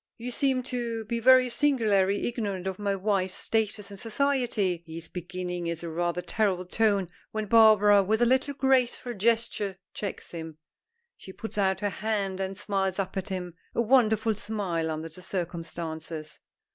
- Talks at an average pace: Yes, average, 170 wpm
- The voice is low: No, high, 200 Hz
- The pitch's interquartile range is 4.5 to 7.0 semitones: No, average, 3.9 semitones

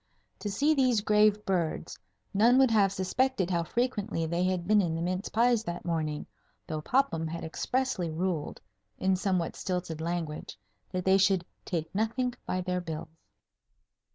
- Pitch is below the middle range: No, medium, 185 Hz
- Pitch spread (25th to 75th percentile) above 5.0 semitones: No, average, 4.1 semitones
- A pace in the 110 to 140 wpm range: No, average, 155 wpm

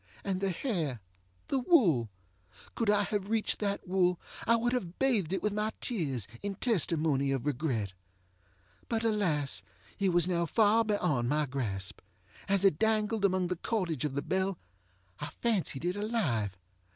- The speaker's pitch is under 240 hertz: Yes, medium, 185 Hz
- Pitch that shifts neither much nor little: No, wide, 6.8 semitones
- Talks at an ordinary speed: Yes, average, 155 wpm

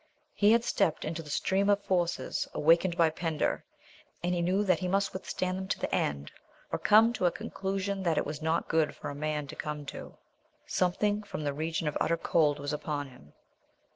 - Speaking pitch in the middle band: Yes, medium, 170 Hz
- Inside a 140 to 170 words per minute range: No, fast, 205 wpm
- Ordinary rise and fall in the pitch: Yes, average, 4.1 semitones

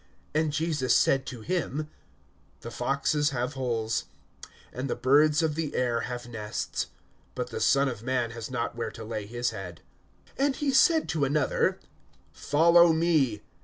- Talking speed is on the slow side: No, average, 160 wpm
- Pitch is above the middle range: No, low, 135 Hz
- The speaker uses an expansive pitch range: No, average, 4.8 semitones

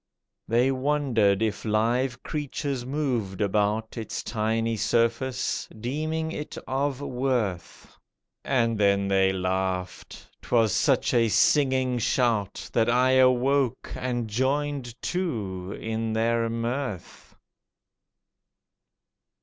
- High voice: No, low, 120 Hz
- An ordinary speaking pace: No, slow, 95 wpm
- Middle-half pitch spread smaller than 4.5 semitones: Yes, average, 3.5 semitones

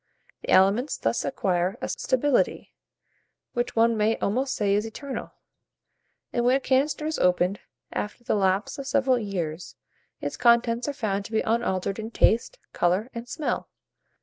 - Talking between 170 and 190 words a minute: No, average, 155 wpm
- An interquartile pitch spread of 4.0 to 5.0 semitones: Yes, average, 4.4 semitones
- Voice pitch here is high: Yes, high, 225 Hz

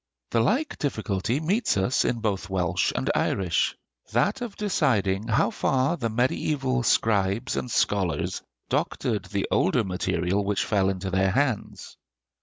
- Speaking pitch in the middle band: No, low, 110 Hz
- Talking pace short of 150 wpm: Yes, average, 140 wpm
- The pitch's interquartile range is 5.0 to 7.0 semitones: Yes, average, 5.3 semitones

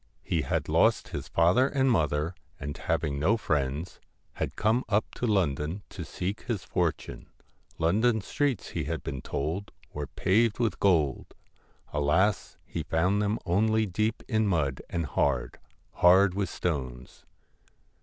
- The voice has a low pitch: Yes, very low, 90 Hz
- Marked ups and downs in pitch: Yes, wide, 6.2 semitones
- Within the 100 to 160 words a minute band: Yes, average, 145 wpm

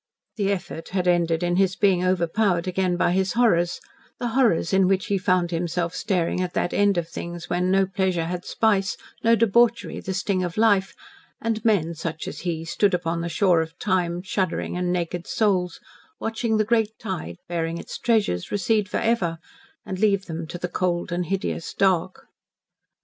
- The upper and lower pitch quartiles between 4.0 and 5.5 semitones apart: No, average, 2.7 semitones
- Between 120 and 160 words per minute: No, average, 180 wpm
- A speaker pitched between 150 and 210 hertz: Yes, medium, 185 Hz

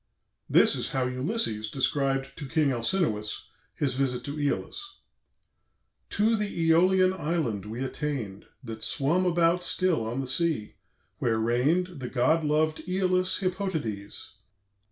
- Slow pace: Yes, slow, 130 wpm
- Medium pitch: Yes, medium, 145 Hz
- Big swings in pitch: Yes, wide, 6.3 semitones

